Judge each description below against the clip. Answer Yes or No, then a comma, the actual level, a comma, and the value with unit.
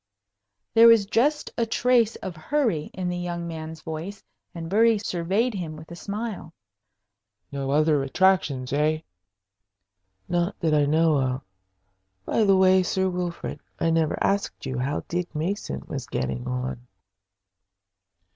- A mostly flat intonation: No, average, 4.5 semitones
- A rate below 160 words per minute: Yes, average, 140 wpm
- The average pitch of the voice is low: No, medium, 170 Hz